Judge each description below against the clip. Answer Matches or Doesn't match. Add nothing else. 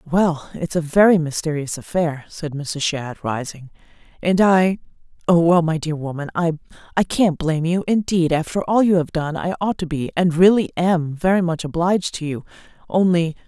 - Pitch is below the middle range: Doesn't match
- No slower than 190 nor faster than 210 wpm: Doesn't match